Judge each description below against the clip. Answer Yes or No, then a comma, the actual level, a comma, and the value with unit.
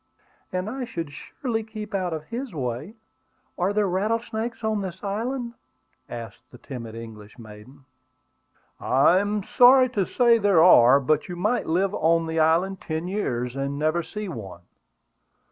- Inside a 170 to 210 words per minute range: No, average, 155 wpm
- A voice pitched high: No, medium, 180 Hz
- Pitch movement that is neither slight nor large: No, wide, 7.2 semitones